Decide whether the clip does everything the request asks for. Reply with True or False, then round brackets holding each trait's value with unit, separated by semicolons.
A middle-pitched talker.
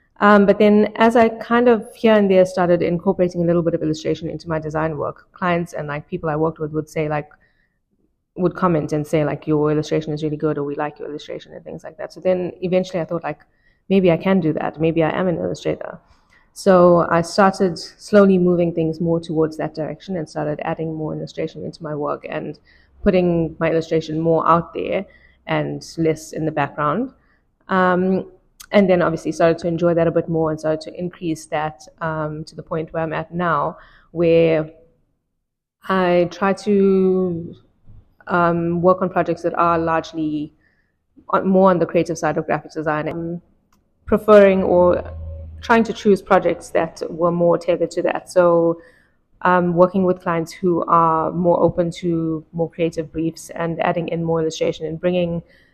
True (170 Hz)